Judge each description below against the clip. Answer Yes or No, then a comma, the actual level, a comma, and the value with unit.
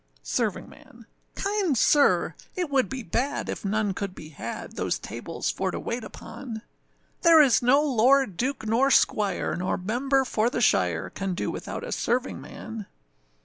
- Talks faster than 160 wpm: No, average, 155 wpm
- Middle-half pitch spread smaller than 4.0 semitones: No, average, 4.7 semitones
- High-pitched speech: Yes, high, 240 Hz